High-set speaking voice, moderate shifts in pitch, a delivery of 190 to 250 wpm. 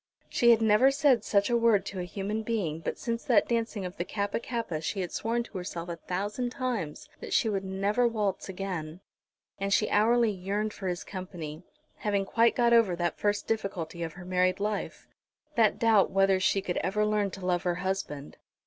Yes: high, 200 Hz; average, 3.6 semitones; average, 200 wpm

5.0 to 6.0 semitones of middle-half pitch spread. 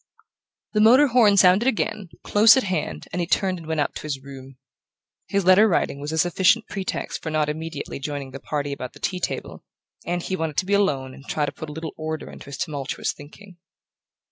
Yes: average, 5.3 semitones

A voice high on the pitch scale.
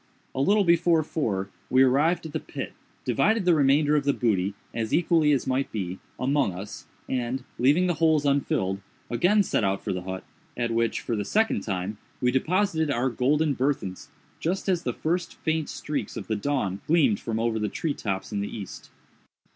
No: low, 135 Hz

